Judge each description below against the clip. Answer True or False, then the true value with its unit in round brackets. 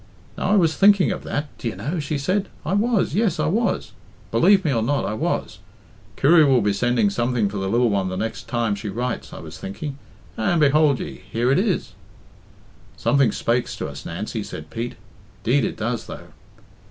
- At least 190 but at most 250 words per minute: True (195 wpm)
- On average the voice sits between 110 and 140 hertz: True (135 Hz)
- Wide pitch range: True (7.0 semitones)